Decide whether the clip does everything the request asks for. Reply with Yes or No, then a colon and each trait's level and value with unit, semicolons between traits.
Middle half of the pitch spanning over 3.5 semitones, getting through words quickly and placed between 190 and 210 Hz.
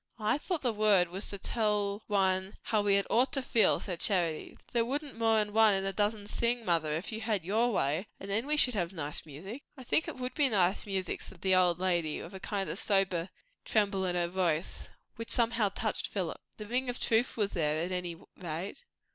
Yes: average, 3.9 semitones; fast, 220 wpm; high, 200 Hz